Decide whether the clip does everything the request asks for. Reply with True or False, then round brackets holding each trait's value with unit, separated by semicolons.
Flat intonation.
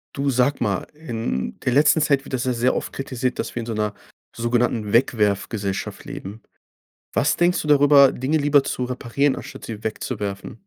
False (4.1 semitones)